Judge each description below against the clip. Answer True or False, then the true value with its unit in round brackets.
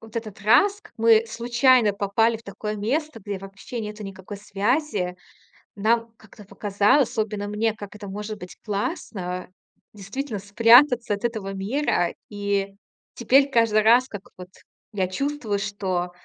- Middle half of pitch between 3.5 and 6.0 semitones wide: False (2.7 semitones)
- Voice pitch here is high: True (210 Hz)